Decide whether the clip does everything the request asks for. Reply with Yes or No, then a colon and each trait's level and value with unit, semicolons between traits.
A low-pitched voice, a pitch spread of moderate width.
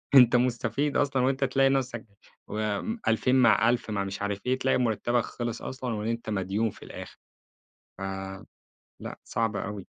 Yes: low, 120 Hz; average, 3.4 semitones